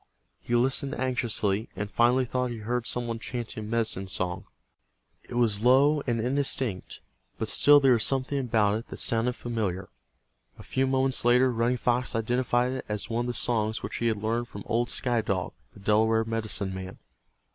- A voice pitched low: Yes, low, 120 Hz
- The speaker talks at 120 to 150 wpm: No, average, 185 wpm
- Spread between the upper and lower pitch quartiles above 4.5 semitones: No, narrow, 2.5 semitones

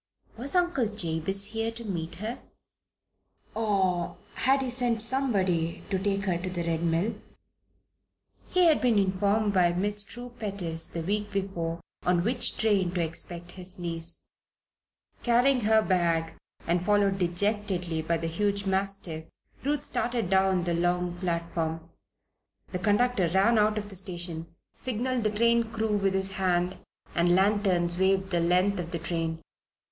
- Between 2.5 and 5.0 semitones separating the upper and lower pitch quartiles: Yes, average, 3.7 semitones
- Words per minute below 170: Yes, average, 150 wpm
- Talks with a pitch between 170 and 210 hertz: Yes, high, 190 Hz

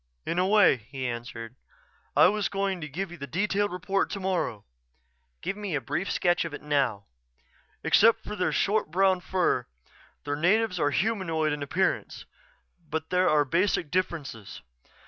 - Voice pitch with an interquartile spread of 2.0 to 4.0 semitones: No, average, 5.2 semitones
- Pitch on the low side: No, medium, 175 Hz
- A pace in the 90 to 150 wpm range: No, average, 160 wpm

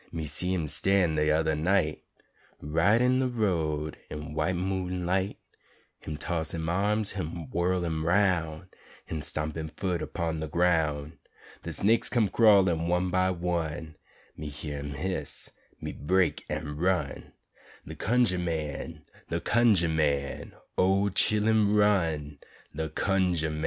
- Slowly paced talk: No, average, 145 wpm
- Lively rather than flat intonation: No, average, 3.5 semitones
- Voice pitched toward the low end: Yes, very low, 85 Hz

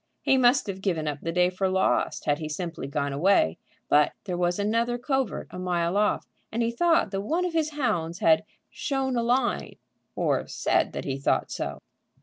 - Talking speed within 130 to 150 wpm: No, average, 195 wpm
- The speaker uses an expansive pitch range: Yes, wide, 6.6 semitones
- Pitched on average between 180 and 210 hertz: Yes, high, 190 Hz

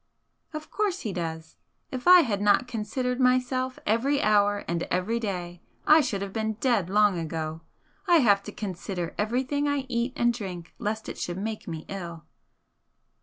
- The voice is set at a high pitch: Yes, high, 210 Hz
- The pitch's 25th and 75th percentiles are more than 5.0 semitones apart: Yes, wide, 5.5 semitones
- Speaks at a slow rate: No, average, 170 wpm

